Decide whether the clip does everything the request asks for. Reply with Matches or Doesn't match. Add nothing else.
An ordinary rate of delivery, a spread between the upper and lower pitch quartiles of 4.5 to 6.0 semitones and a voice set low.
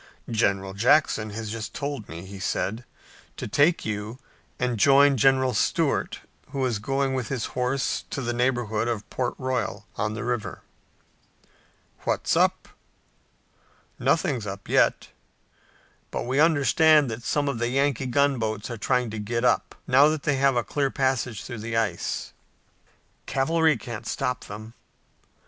Doesn't match